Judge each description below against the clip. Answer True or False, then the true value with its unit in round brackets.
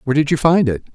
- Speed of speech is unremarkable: False (315 wpm)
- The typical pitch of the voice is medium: True (145 Hz)